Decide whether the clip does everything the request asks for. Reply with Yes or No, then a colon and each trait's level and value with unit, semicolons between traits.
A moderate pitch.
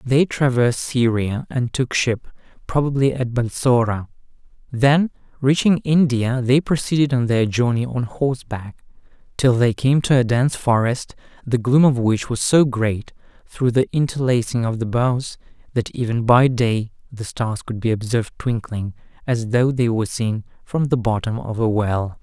No: low, 120 Hz